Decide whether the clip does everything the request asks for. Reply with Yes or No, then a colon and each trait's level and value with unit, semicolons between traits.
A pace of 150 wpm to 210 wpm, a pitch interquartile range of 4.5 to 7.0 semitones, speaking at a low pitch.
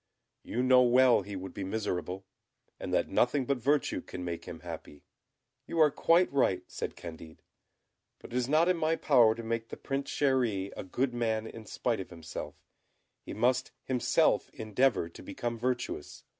Yes: average, 175 wpm; average, 5.0 semitones; low, 120 Hz